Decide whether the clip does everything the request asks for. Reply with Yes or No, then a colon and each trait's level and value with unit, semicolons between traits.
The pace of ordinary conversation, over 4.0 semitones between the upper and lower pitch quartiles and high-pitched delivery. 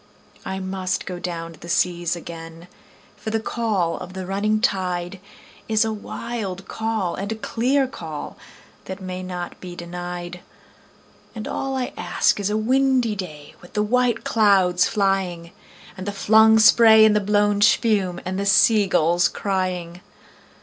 No: average, 155 wpm; average, 3.5 semitones; high, 195 Hz